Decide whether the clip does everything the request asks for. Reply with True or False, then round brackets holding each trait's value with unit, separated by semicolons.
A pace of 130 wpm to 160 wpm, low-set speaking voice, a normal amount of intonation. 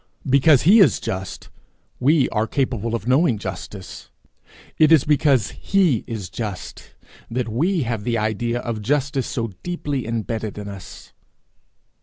True (140 wpm; 120 Hz; 4.8 semitones)